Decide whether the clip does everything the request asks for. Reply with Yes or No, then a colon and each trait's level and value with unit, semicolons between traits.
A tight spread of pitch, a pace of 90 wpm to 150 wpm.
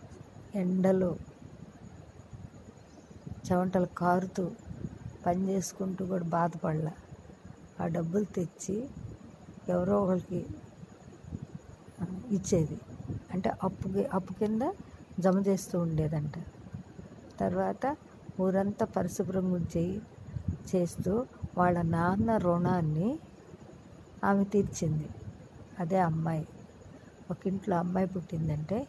No: narrow, 2.1 semitones; average, 75 wpm